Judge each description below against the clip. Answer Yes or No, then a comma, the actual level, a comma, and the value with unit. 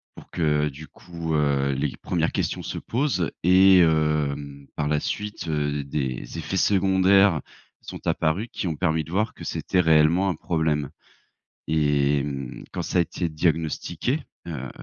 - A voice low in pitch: Yes, very low, 80 Hz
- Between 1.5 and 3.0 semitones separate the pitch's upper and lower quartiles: No, average, 3.7 semitones